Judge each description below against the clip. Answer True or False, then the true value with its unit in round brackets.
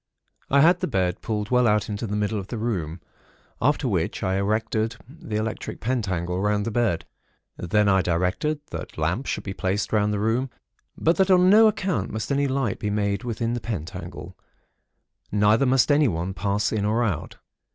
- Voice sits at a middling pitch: False (105 Hz)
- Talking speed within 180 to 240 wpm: True (185 wpm)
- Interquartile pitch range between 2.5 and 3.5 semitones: False (4.0 semitones)